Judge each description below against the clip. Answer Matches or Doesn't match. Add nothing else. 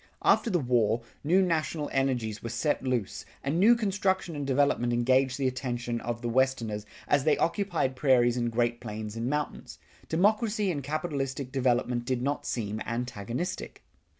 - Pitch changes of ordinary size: Matches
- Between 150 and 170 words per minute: Matches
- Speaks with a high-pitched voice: Doesn't match